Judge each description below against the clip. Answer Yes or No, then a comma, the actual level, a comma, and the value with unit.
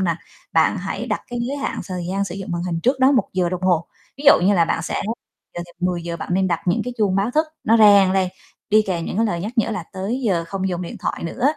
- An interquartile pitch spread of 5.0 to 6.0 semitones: No, average, 3.8 semitones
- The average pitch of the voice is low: No, high, 190 Hz